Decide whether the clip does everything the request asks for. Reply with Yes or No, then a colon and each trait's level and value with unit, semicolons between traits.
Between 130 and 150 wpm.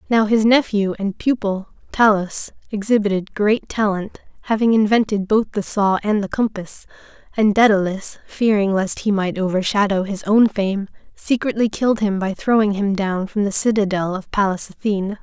No: average, 160 wpm